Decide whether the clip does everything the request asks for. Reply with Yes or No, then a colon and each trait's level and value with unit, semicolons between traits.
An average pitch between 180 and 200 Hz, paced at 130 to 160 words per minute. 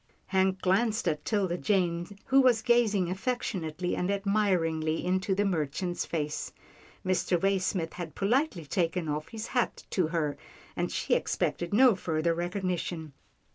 Yes: medium, 185 Hz; slow, 135 wpm